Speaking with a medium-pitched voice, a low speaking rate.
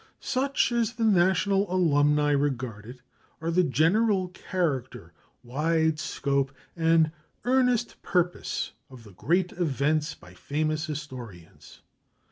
Yes: medium, 155 Hz; slow, 110 wpm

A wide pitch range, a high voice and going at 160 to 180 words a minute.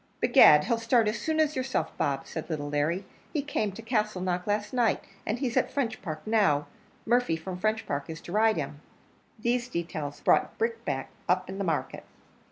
Yes: wide, 6.4 semitones; high, 205 Hz; average, 175 wpm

